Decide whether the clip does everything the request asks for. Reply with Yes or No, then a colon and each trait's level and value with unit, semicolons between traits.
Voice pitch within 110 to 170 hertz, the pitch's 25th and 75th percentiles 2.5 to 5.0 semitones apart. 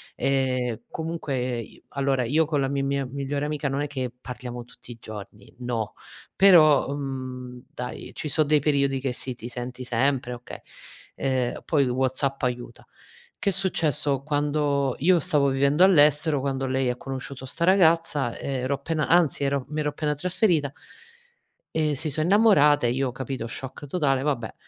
Yes: medium, 140 Hz; average, 2.9 semitones